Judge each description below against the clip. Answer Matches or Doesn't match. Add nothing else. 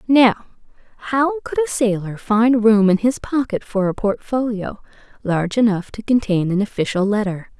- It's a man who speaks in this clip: Doesn't match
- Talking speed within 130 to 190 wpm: Matches